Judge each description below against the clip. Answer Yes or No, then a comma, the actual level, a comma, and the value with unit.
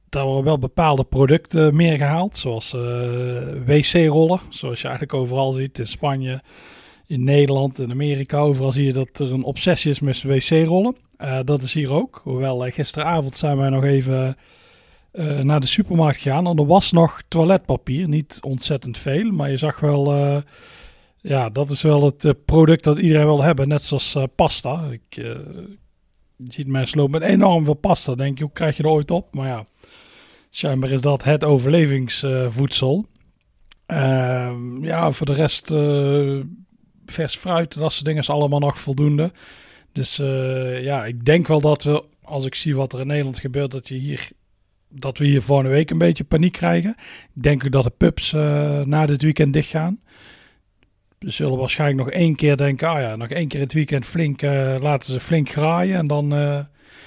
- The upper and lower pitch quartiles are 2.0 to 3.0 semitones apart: Yes, average, 2.7 semitones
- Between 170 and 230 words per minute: Yes, average, 190 wpm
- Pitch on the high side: No, medium, 145 Hz